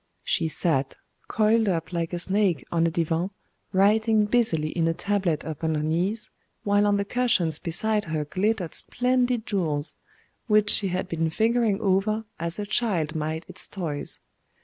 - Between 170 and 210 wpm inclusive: No, average, 160 wpm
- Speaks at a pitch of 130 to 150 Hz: No, medium, 185 Hz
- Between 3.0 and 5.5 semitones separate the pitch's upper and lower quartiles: Yes, average, 4.6 semitones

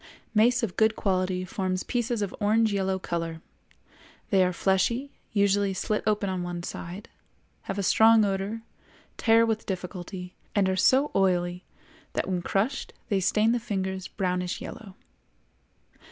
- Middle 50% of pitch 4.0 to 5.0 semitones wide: No, average, 3.0 semitones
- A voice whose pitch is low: No, high, 195 Hz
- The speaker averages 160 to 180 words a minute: No, average, 145 wpm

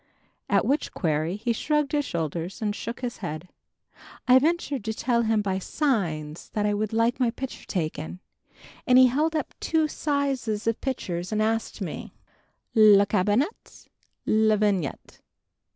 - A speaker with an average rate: Yes, average, 150 wpm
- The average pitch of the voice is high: Yes, high, 220 Hz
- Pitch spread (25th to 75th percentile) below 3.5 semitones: No, average, 5.2 semitones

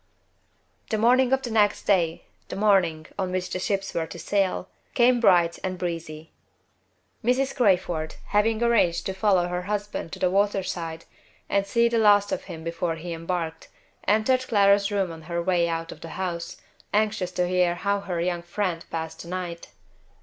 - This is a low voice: No, medium, 185 Hz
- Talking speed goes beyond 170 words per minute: Yes, average, 180 wpm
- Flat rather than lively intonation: No, average, 3.4 semitones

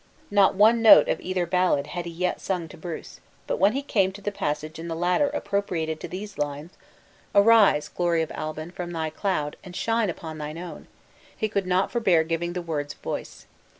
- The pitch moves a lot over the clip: No, average, 3.7 semitones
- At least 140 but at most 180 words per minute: No, average, 200 wpm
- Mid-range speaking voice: Yes, medium, 175 Hz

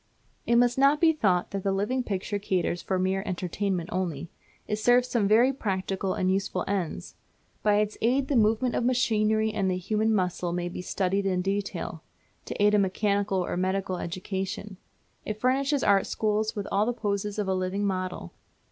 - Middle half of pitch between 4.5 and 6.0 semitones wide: No, average, 2.7 semitones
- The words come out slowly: No, average, 185 wpm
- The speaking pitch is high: Yes, high, 200 Hz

